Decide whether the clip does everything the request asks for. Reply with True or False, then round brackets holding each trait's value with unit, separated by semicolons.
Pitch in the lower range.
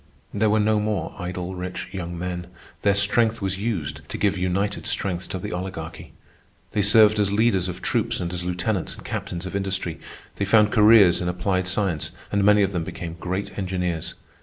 True (95 Hz)